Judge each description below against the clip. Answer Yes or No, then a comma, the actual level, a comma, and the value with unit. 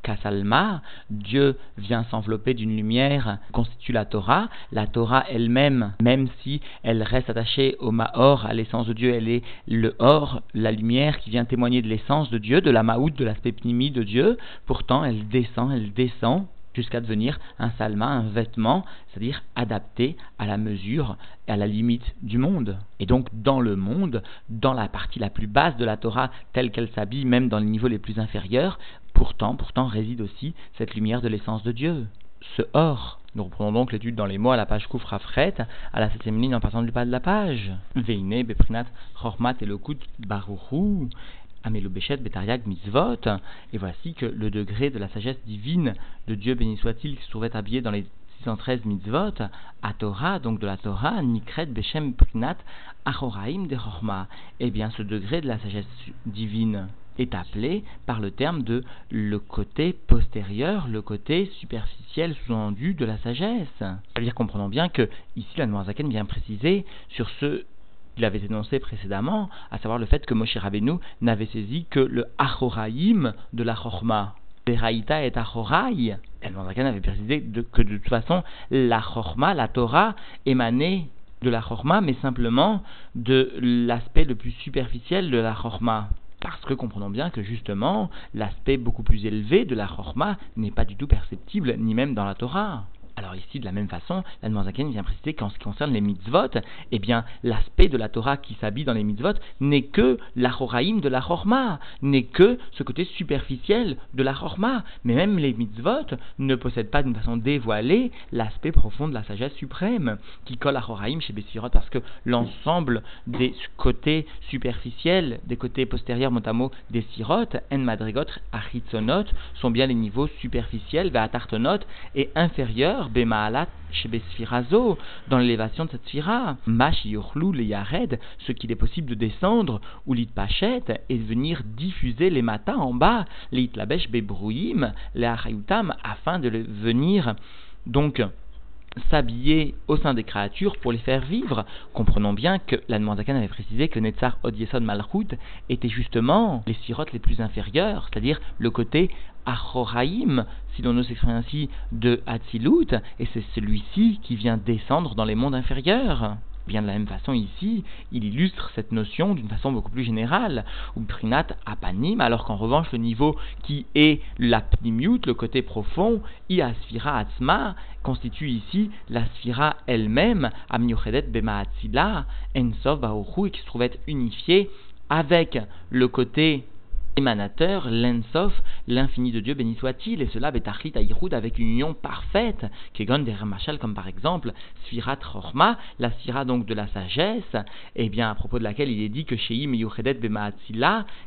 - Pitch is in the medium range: No, low, 120 Hz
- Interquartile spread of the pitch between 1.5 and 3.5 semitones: No, average, 3.9 semitones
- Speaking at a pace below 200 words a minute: Yes, average, 165 wpm